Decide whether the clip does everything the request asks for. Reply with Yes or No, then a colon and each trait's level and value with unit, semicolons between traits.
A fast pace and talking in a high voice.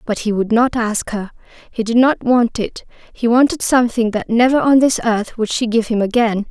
Yes: fast, 220 wpm; high, 230 Hz